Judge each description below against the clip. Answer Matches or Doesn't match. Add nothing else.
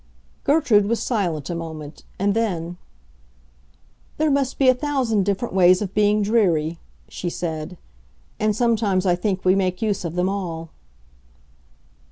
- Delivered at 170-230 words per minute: Doesn't match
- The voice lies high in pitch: Matches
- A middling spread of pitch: Matches